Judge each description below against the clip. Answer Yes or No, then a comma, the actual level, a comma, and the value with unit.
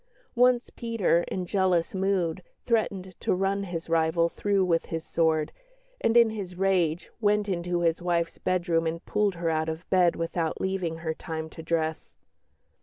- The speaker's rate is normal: Yes, average, 165 wpm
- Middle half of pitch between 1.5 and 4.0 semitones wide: Yes, average, 2.8 semitones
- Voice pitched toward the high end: No, medium, 175 Hz